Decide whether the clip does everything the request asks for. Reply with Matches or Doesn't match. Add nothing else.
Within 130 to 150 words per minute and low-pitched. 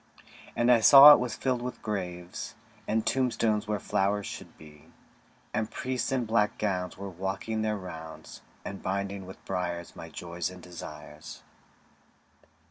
Matches